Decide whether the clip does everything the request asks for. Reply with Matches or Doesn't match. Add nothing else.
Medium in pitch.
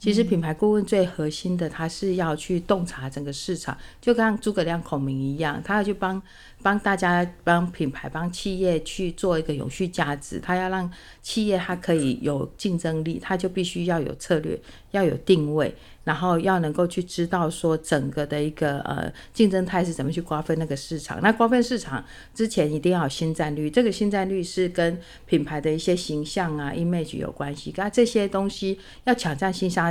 Matches